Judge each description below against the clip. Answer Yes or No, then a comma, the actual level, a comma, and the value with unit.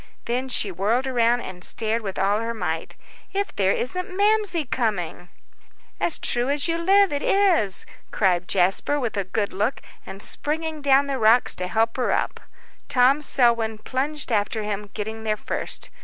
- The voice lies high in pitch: Yes, high, 235 Hz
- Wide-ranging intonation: Yes, wide, 5.8 semitones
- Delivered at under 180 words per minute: Yes, average, 170 wpm